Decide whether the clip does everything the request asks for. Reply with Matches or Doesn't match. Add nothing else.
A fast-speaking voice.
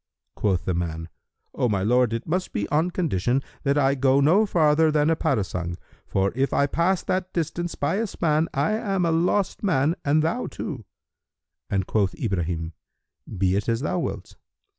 Doesn't match